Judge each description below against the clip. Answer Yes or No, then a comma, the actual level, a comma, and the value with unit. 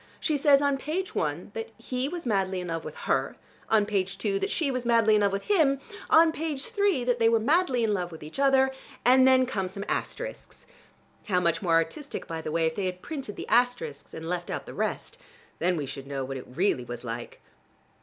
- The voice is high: Yes, high, 225 Hz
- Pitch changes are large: Yes, wide, 8.0 semitones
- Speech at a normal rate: No, fast, 225 wpm